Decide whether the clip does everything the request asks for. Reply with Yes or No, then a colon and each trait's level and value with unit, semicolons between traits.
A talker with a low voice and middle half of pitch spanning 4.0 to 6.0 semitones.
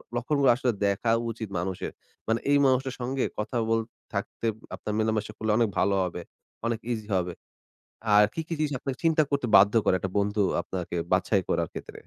Yes: low, 110 Hz; average, 4.4 semitones